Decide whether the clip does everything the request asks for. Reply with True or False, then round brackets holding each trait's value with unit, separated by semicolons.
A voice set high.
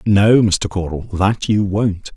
False (100 Hz)